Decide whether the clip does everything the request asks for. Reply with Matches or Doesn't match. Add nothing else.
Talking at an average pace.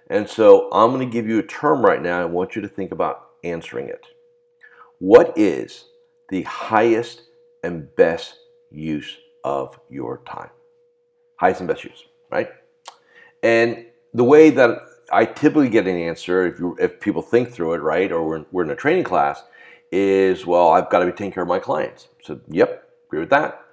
Matches